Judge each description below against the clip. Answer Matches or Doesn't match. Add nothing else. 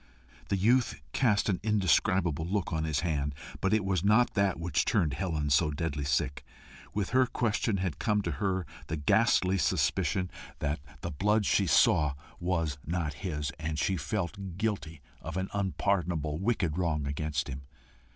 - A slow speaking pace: Doesn't match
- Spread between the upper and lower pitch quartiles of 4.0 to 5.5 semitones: Matches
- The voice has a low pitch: Matches